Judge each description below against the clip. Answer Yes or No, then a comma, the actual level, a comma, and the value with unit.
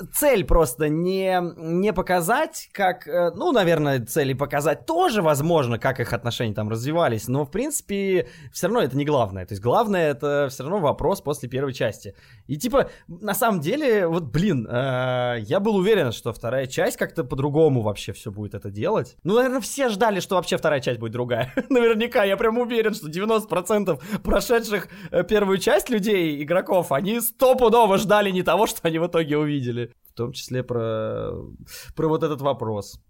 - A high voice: No, medium, 165 Hz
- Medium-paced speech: No, fast, 170 wpm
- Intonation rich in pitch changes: Yes, wide, 7.8 semitones